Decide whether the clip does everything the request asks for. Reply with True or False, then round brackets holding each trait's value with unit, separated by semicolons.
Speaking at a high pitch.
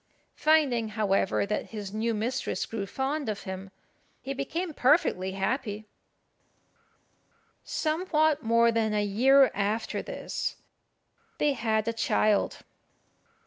True (230 Hz)